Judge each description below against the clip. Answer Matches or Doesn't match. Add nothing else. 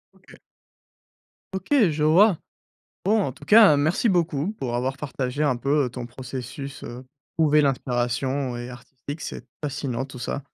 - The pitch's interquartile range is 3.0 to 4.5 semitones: Matches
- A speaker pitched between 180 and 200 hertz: Doesn't match